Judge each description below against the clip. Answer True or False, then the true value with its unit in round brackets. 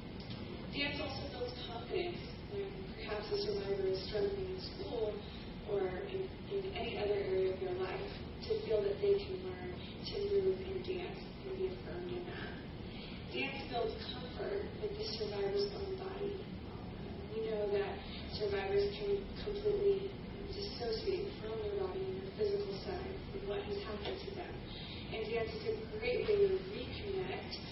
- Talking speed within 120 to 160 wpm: True (155 wpm)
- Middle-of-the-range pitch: False (215 Hz)